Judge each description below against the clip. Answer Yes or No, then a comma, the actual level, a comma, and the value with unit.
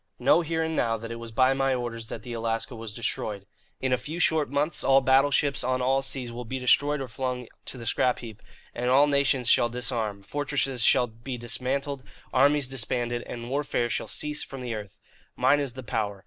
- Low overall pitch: Yes, low, 125 Hz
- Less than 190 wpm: No, fast, 205 wpm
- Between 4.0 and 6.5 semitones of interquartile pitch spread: No, average, 2.7 semitones